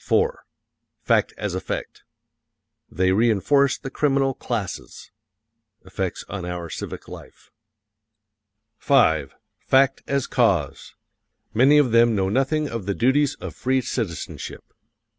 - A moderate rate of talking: No, slow, 110 wpm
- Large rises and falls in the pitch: Yes, wide, 6.2 semitones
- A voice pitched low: Yes, low, 120 Hz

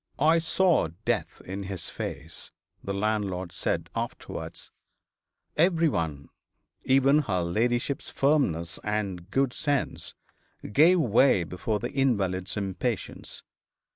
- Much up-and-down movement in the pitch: Yes, wide, 7.1 semitones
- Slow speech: Yes, slow, 105 wpm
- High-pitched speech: No, low, 105 Hz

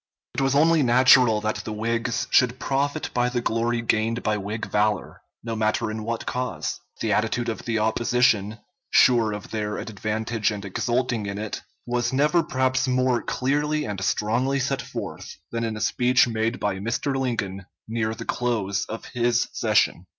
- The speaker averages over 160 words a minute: Yes, average, 170 wpm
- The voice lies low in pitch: Yes, low, 115 Hz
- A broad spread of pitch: No, average, 2.9 semitones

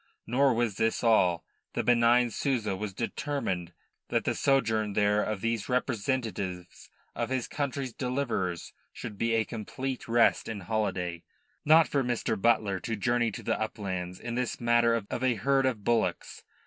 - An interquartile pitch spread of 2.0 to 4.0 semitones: Yes, average, 3.5 semitones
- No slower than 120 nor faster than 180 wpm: Yes, average, 160 wpm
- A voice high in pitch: No, low, 115 Hz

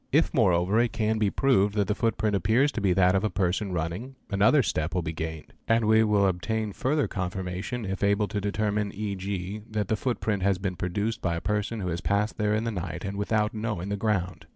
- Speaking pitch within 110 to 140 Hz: No, low, 100 Hz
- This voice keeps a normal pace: No, fast, 225 wpm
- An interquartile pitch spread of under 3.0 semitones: Yes, narrow, 2.6 semitones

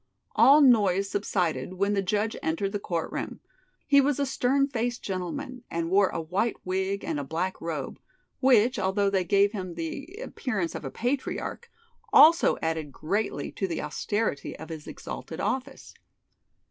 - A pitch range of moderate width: No, wide, 6.4 semitones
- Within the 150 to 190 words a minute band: Yes, average, 160 wpm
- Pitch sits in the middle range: No, high, 200 Hz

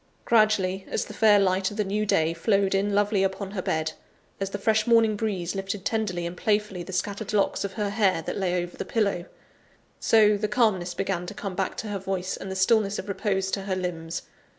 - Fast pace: Yes, fast, 220 wpm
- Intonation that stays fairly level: Yes, narrow, 2.2 semitones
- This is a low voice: No, high, 195 Hz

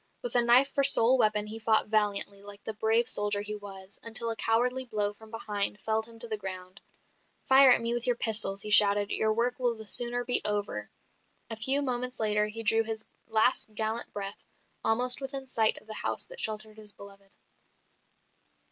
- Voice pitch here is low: No, high, 220 Hz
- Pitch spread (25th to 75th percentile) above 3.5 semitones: No, narrow, 2.5 semitones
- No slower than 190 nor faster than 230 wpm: Yes, average, 195 wpm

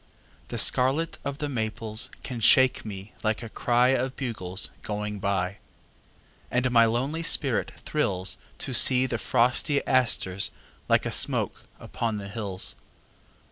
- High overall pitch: No, low, 115 Hz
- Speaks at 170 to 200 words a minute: No, average, 140 wpm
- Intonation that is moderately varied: Yes, average, 3.8 semitones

